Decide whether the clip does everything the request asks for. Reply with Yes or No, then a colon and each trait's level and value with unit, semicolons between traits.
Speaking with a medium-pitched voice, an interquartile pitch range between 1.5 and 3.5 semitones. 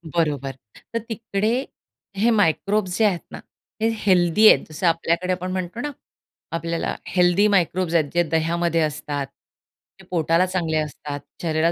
Yes: medium, 170 Hz; narrow, 2.6 semitones